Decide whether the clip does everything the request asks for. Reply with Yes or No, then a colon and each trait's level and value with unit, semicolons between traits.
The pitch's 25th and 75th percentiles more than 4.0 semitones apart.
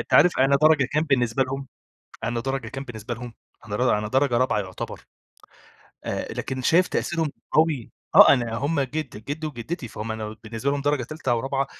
No: average, 3.7 semitones